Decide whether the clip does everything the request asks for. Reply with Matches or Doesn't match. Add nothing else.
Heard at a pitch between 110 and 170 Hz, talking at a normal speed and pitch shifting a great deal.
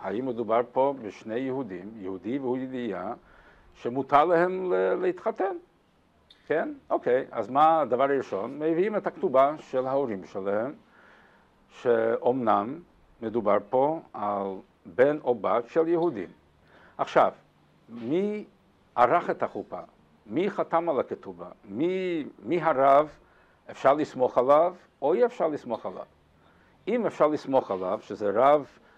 Matches